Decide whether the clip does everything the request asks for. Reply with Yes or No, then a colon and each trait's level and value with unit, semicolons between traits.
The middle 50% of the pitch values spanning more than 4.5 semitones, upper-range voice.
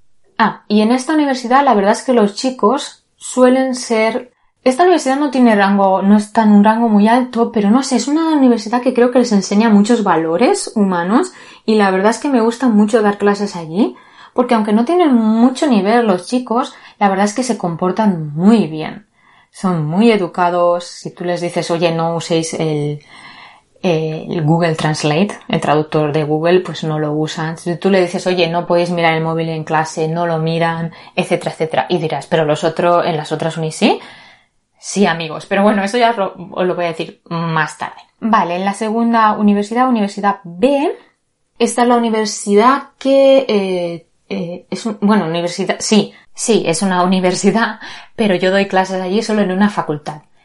Yes: average, 5.2 semitones; high, 200 Hz